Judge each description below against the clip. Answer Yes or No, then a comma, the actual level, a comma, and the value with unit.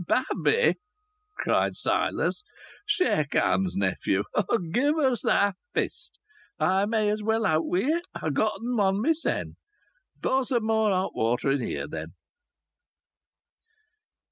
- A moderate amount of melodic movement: No, wide, 5.9 semitones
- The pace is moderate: No, slow, 120 wpm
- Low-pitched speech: No, high, 215 Hz